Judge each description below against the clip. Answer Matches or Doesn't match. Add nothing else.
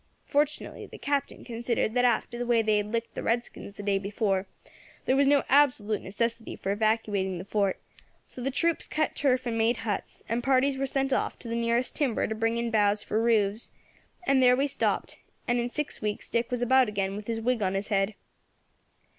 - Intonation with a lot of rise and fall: Doesn't match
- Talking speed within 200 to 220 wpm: Matches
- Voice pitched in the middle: Doesn't match